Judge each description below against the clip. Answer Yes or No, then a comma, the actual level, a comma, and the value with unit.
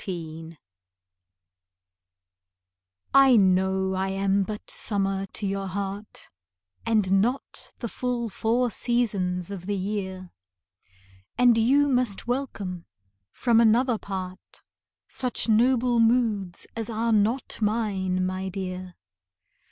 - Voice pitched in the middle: No, high, 205 Hz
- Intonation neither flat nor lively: Yes, average, 3.8 semitones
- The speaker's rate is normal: No, slow, 105 wpm